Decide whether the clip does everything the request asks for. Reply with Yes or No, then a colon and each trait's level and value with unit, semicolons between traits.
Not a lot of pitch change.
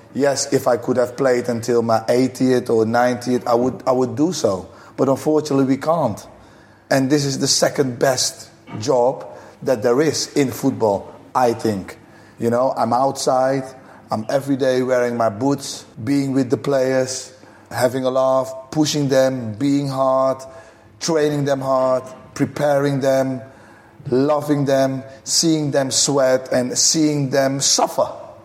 Yes: narrow, 1.8 semitones